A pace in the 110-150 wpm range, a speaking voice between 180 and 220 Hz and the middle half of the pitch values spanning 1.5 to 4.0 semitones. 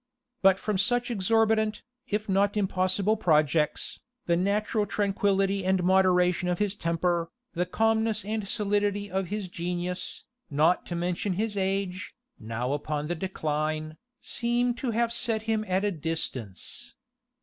Yes: average, 140 wpm; high, 190 Hz; average, 3.4 semitones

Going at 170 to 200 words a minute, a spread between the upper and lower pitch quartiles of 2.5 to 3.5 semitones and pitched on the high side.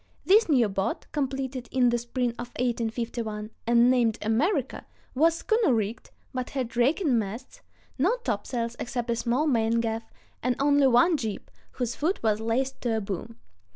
No: average, 160 wpm; average, 2.9 semitones; high, 240 Hz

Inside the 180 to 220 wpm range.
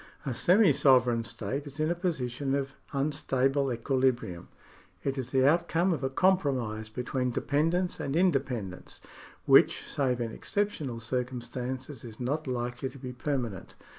No: average, 155 wpm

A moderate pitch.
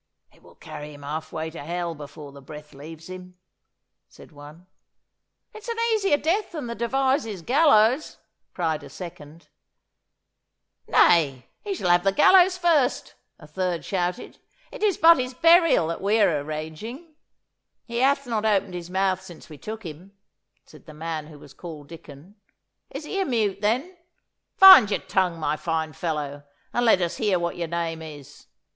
Yes: medium, 180 Hz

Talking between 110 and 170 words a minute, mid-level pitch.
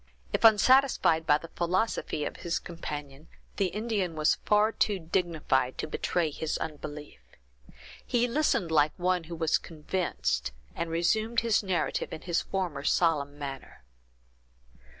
Yes: slow, 135 wpm; medium, 170 Hz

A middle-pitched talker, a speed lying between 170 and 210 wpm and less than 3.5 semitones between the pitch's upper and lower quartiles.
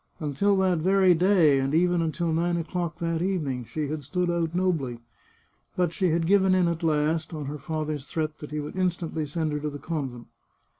Yes: medium, 165 Hz; average, 200 wpm; average, 2.9 semitones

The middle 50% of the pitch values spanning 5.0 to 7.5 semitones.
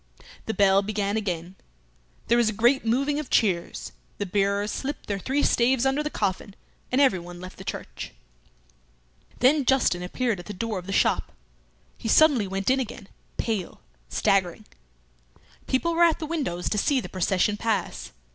Yes: wide, 5.4 semitones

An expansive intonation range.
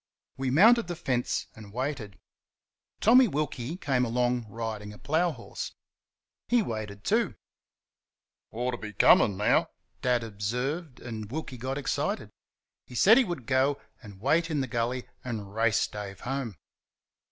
No: average, 4.8 semitones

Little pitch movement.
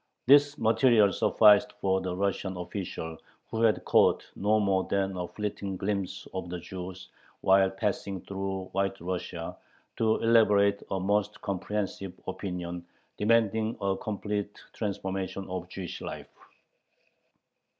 Yes: narrow, 2.1 semitones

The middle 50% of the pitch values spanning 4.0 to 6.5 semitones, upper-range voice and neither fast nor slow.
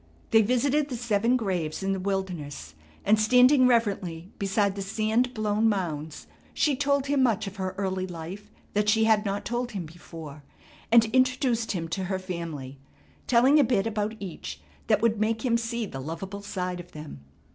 Yes: average, 4.3 semitones; high, 205 Hz; average, 180 wpm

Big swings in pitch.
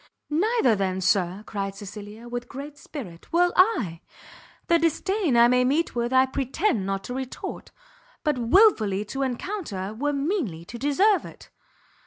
Yes: wide, 7.7 semitones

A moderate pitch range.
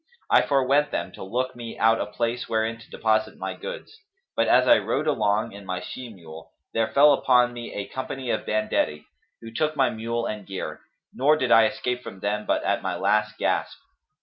Yes: average, 3.4 semitones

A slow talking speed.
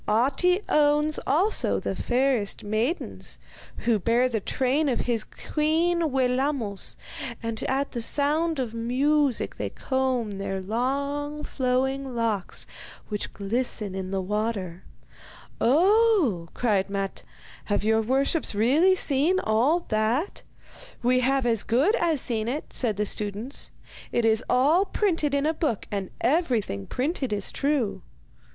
Yes: slow, 130 wpm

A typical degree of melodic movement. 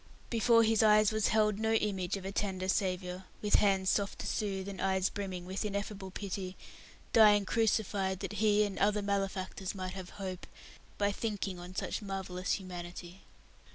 No: narrow, 1.9 semitones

